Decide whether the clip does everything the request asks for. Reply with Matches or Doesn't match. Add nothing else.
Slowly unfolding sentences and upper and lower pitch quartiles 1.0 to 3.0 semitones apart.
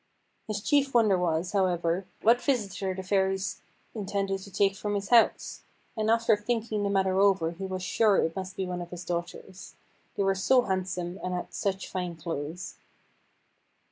Doesn't match